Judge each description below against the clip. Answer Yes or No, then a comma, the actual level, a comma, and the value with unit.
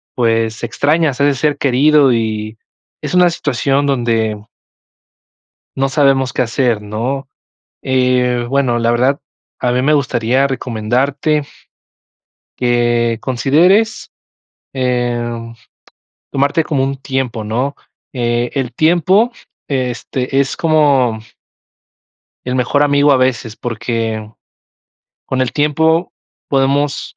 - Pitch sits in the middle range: No, low, 130 Hz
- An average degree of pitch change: Yes, average, 3.1 semitones